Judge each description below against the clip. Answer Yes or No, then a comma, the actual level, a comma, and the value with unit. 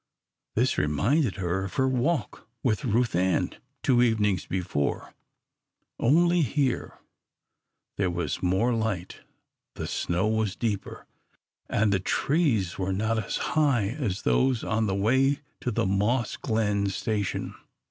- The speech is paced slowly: Yes, slow, 130 wpm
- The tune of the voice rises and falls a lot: No, average, 4.7 semitones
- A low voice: Yes, low, 110 Hz